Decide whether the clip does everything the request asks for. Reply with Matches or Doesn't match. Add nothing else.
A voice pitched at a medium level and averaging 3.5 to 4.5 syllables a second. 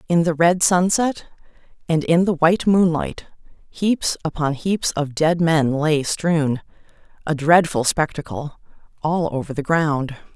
Matches